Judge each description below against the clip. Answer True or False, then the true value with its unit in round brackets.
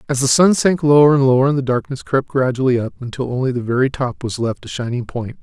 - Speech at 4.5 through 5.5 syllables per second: False (6.0 syllables/s)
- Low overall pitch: True (130 Hz)